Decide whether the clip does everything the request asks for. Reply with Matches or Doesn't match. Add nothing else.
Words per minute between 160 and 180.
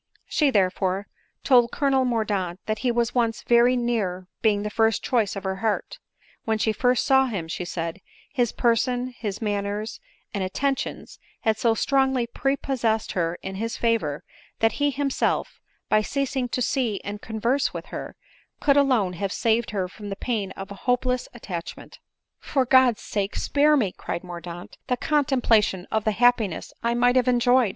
Matches